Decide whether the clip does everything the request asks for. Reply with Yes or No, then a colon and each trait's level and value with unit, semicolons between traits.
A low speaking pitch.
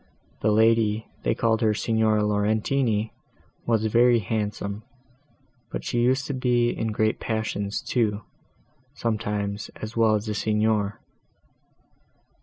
Yes: low, 110 Hz